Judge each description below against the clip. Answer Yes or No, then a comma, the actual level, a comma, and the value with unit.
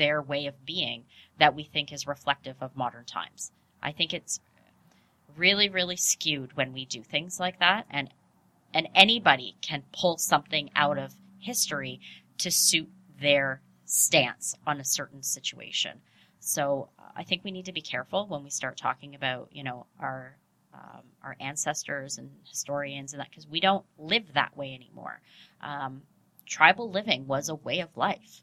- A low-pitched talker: No, medium, 145 Hz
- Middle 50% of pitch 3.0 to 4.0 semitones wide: No, average, 4.9 semitones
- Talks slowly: No, average, 165 wpm